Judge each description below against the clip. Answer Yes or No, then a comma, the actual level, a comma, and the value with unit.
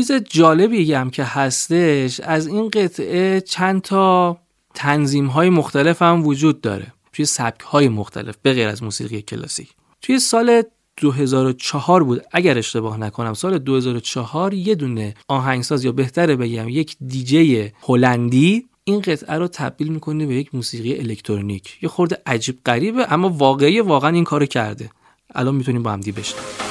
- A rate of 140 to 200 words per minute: Yes, average, 150 wpm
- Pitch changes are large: Yes, wide, 6.0 semitones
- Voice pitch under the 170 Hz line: Yes, medium, 140 Hz